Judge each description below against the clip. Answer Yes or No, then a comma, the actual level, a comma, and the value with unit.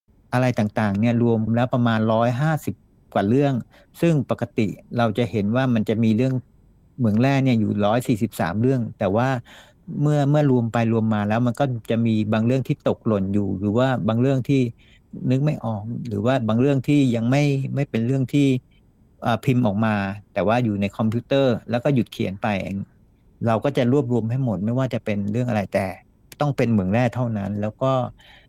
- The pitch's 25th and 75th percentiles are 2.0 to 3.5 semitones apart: Yes, average, 3.2 semitones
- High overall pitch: No, low, 120 Hz